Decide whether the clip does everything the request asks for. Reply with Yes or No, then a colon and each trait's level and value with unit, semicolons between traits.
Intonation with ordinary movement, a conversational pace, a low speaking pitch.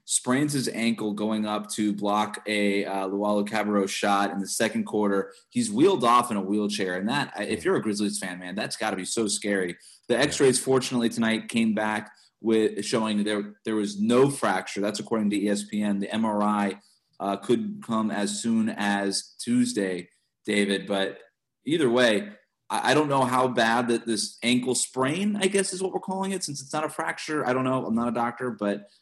Yes: average, 3.4 semitones; average, 190 wpm; low, 105 Hz